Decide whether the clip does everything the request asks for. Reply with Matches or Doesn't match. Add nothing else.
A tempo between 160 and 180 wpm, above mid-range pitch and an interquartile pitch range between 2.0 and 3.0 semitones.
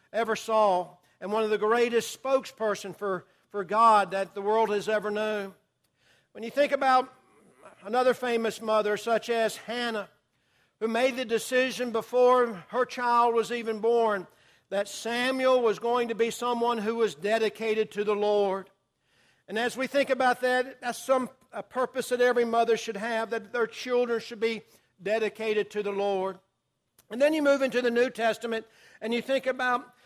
Matches